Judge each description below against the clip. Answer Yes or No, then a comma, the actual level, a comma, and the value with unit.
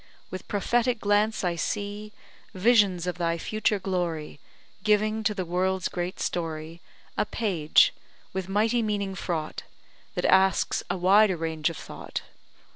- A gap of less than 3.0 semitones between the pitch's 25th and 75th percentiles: No, average, 3.3 semitones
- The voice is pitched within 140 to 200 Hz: Yes, high, 190 Hz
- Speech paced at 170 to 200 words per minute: No, slow, 135 wpm